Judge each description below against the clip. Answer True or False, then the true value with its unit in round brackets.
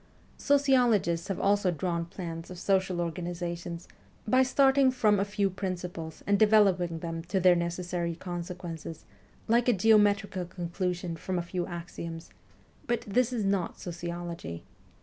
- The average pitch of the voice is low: False (180 Hz)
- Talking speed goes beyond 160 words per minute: False (135 wpm)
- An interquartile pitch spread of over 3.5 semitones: False (3.0 semitones)